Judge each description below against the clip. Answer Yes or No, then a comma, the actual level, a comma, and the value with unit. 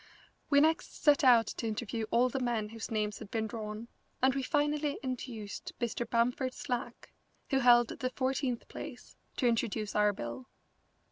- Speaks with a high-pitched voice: Yes, high, 240 Hz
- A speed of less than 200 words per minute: Yes, average, 160 wpm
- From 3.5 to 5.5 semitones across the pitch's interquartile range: No, average, 3.1 semitones